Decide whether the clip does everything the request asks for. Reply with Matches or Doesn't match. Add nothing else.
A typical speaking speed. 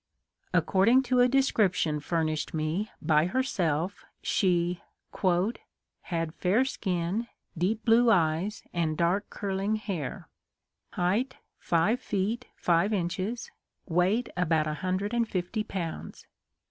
Doesn't match